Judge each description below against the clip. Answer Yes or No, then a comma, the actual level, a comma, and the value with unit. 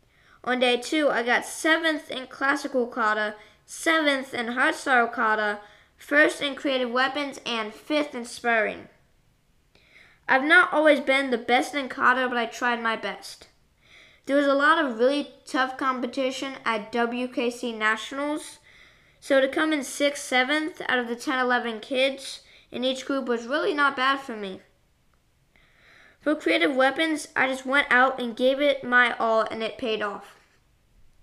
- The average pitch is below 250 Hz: No, very high, 260 Hz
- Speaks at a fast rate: No, average, 155 wpm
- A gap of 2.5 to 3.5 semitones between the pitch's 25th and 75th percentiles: Yes, average, 3.1 semitones